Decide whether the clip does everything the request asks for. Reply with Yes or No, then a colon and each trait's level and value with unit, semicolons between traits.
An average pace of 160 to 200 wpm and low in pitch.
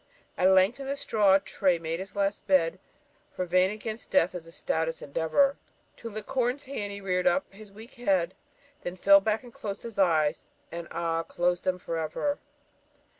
No: average, 180 wpm; high, 190 Hz